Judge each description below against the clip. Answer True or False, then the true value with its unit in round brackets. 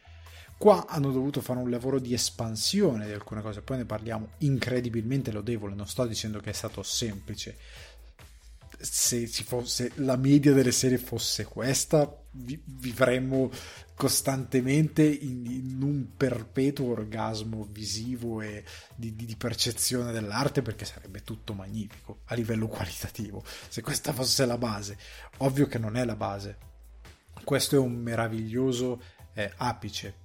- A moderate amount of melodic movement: True (3.4 semitones)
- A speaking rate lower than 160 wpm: True (140 wpm)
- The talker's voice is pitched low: True (120 Hz)